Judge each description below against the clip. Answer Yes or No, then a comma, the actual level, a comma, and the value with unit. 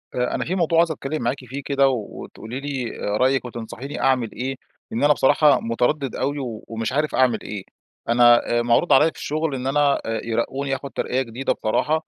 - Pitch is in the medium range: No, low, 130 Hz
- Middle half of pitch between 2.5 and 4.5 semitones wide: Yes, average, 3.4 semitones